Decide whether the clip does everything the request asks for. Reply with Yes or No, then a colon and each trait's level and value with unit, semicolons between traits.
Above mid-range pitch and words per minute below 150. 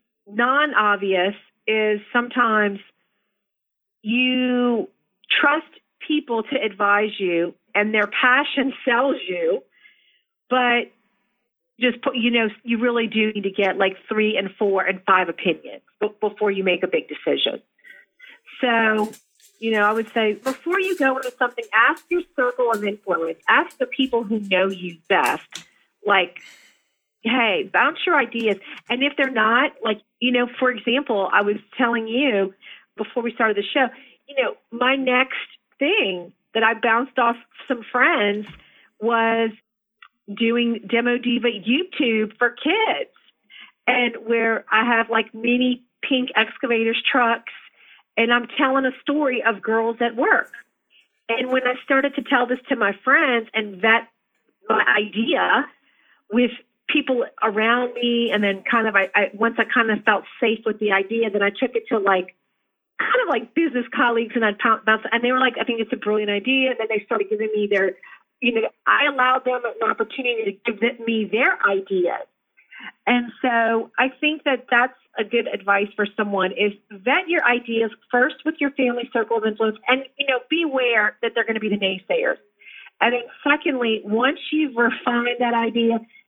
No: high, 235 Hz; average, 165 wpm